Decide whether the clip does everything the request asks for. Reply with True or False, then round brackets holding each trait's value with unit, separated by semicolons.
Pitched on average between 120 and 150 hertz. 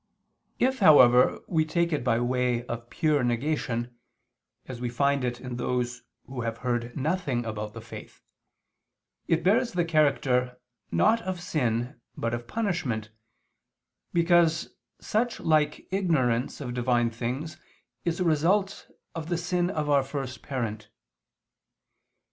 True (135 Hz)